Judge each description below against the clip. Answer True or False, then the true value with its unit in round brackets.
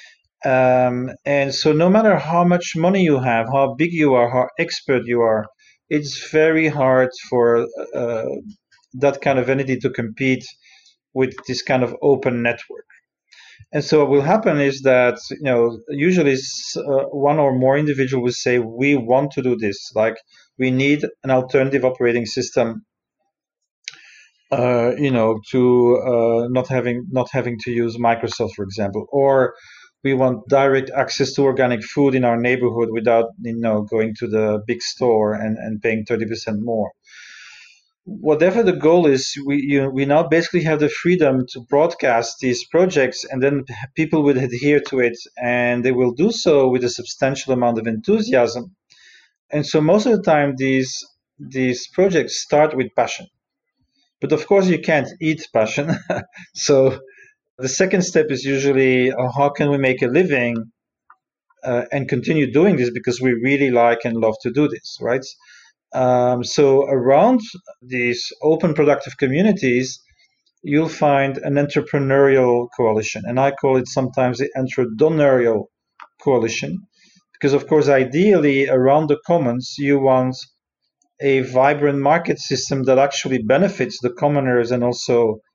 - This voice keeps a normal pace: True (155 wpm)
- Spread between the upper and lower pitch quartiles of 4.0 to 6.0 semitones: False (3.1 semitones)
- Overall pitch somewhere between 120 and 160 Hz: True (135 Hz)